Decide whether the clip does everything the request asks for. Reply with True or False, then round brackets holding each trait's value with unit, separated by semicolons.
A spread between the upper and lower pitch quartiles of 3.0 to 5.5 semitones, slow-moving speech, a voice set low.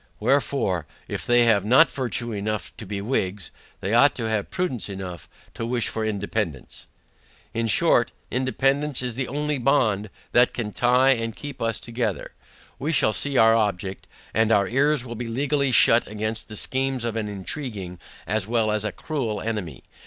False (3.8 semitones; 175 wpm; 115 Hz)